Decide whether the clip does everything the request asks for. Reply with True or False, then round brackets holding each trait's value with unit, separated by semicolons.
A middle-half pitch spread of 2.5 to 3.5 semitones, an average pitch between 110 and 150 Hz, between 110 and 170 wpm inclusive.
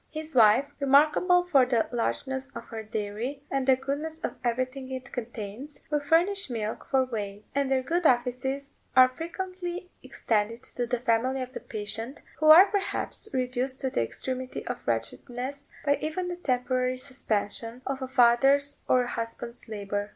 False (3.2 semitones; 255 Hz; 165 wpm)